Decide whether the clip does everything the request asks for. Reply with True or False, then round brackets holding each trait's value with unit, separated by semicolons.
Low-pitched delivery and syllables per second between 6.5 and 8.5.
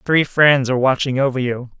False (130 Hz; 5.6 syllables/s)